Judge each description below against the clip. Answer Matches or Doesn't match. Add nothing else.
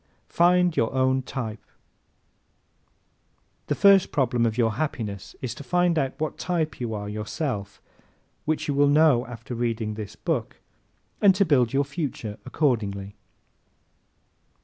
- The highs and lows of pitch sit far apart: Matches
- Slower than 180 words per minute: Matches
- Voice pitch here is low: Matches